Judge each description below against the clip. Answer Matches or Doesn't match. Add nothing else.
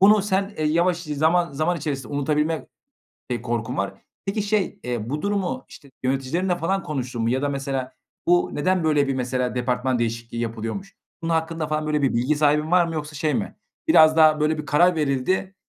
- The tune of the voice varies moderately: Matches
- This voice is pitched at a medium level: Matches